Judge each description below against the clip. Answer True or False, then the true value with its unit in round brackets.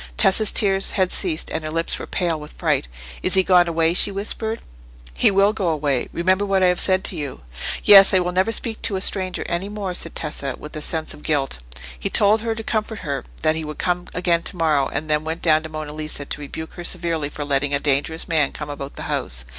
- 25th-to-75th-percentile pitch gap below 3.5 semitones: False (4.0 semitones)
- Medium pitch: True (165 Hz)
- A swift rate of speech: True (240 wpm)